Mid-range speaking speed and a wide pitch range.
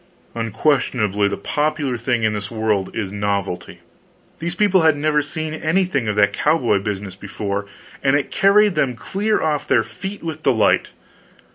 Yes: average, 155 wpm; wide, 7.2 semitones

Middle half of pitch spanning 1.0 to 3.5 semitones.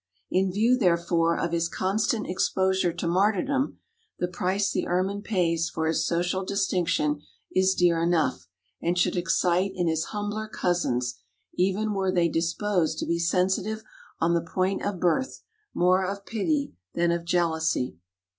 Yes: average, 2.7 semitones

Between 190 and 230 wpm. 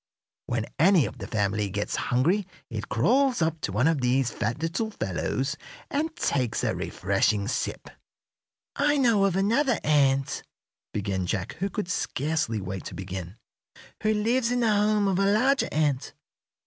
No: average, 160 wpm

